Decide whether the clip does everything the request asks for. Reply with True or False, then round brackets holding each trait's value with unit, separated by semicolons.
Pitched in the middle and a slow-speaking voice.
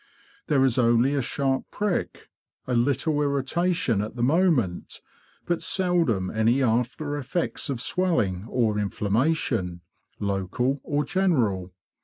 False (130 Hz; 120 wpm)